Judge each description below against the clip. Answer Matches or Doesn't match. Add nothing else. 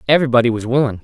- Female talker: Doesn't match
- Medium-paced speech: Matches